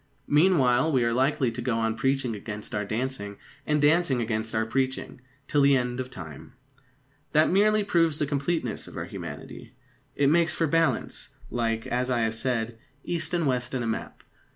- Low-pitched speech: Yes, low, 130 Hz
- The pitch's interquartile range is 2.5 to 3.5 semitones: No, average, 4.8 semitones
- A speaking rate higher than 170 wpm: Yes, average, 180 wpm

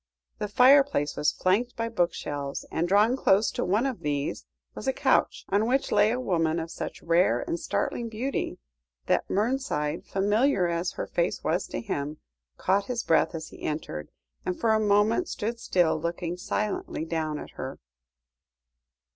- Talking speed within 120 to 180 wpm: Yes, average, 165 wpm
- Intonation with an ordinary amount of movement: No, wide, 6.1 semitones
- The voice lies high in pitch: Yes, high, 200 Hz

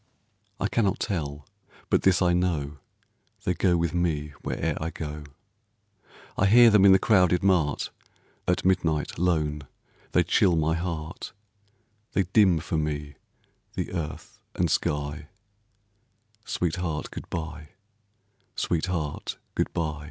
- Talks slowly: Yes, slow, 125 wpm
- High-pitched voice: No, very low, 85 Hz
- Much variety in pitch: No, average, 3.2 semitones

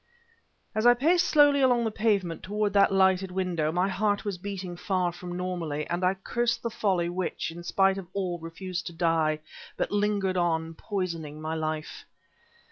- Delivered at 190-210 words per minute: No, average, 175 wpm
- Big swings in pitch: No, average, 3.1 semitones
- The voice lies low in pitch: No, medium, 185 Hz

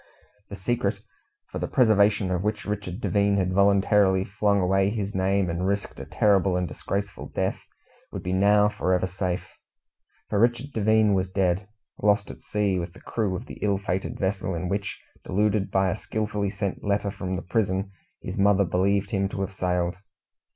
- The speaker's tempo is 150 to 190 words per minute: Yes, average, 180 wpm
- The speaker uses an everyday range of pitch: No, narrow, 1.7 semitones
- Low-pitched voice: Yes, low, 100 Hz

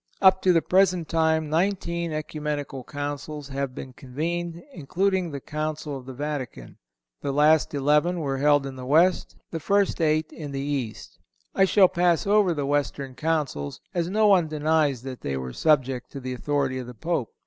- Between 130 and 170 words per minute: No, average, 180 wpm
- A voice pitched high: No, medium, 150 Hz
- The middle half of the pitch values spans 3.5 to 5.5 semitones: Yes, average, 3.8 semitones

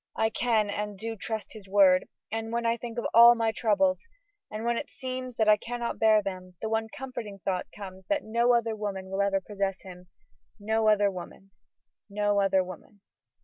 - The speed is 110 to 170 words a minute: No, average, 190 wpm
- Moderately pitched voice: No, high, 215 Hz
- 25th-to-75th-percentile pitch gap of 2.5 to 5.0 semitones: Yes, average, 2.9 semitones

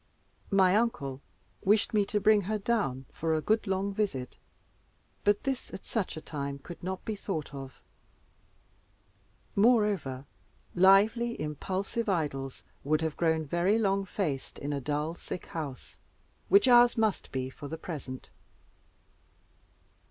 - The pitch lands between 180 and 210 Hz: Yes, medium, 185 Hz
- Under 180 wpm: Yes, slow, 135 wpm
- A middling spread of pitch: No, wide, 6.2 semitones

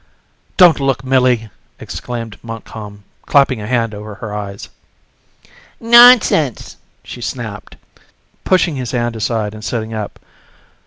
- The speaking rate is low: Yes, slow, 115 wpm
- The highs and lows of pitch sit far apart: No, average, 3.9 semitones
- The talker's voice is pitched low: Yes, low, 115 Hz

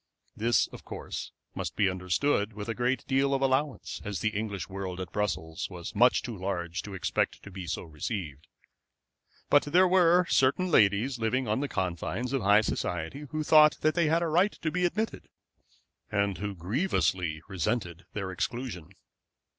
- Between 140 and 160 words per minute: No, average, 170 wpm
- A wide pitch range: Yes, wide, 6.9 semitones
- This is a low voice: Yes, low, 105 Hz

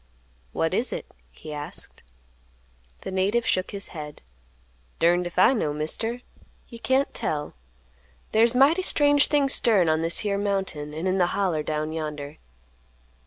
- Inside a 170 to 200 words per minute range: No, average, 150 wpm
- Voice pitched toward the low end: No, medium, 185 Hz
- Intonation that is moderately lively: No, wide, 7.0 semitones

